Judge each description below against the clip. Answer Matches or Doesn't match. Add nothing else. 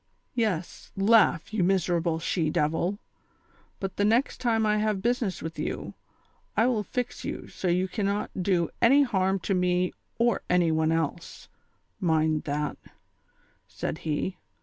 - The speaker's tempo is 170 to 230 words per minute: Doesn't match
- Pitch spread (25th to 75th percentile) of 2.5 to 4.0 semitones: Doesn't match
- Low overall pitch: Doesn't match